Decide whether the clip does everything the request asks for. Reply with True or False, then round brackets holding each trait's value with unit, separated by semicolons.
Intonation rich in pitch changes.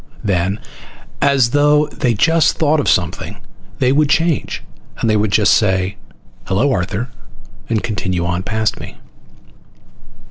True (7.0 semitones)